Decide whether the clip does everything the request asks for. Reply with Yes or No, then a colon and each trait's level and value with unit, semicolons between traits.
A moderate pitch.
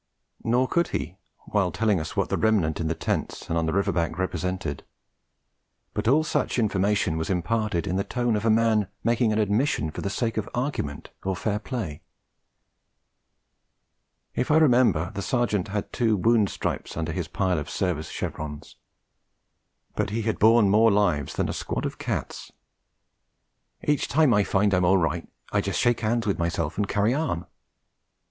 No: low, 100 Hz